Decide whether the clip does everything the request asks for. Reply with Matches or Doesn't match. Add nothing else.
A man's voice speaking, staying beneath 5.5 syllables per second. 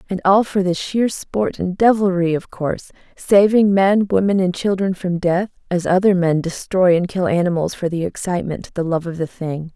Doesn't match